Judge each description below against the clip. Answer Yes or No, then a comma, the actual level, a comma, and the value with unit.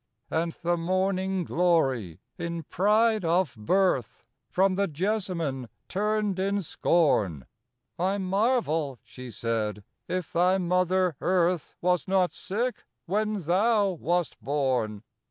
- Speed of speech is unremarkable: No, slow, 120 wpm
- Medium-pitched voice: Yes, medium, 180 Hz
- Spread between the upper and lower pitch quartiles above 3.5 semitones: Yes, average, 4.4 semitones